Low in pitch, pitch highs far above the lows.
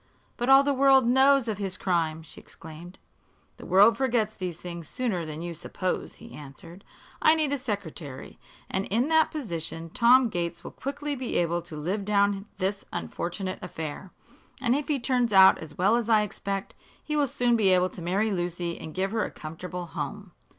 No: high, 195 Hz; wide, 6.0 semitones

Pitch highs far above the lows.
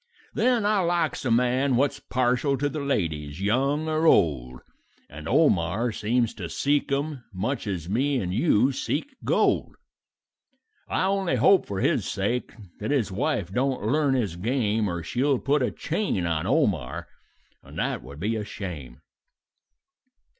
Yes: wide, 6.8 semitones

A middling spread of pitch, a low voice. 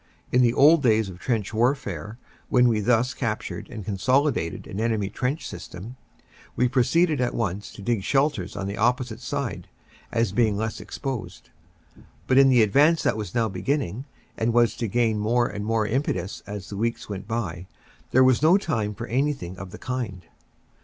Yes: average, 3.9 semitones; low, 115 Hz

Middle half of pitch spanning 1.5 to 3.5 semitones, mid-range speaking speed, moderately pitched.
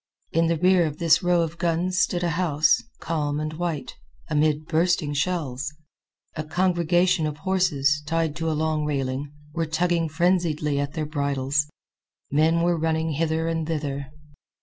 Yes: narrow, 2.4 semitones; average, 155 wpm; medium, 160 Hz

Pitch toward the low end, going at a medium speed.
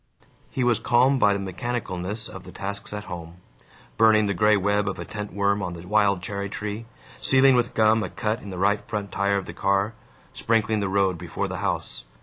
No: low, 100 Hz; fast, 210 wpm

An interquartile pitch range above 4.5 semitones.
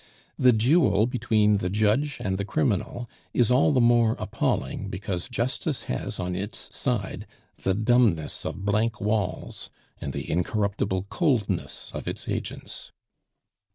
No: average, 3.9 semitones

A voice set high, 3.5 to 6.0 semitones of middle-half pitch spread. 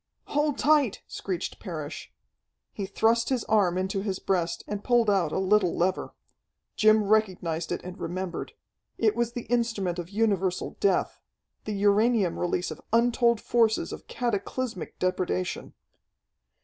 Yes: high, 205 Hz; average, 4.0 semitones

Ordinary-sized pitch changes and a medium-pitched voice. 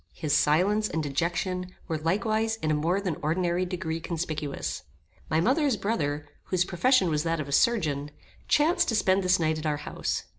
Yes: average, 4.3 semitones; medium, 175 Hz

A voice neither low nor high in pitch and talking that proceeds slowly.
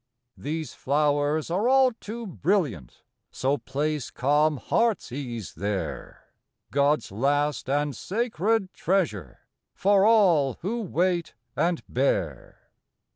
Yes: medium, 150 Hz; slow, 105 wpm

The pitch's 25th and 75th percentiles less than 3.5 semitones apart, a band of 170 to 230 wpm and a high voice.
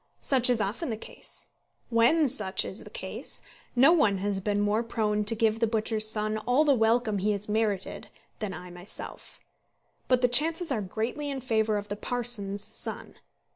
Yes: average, 3.1 semitones; average, 180 wpm; high, 220 Hz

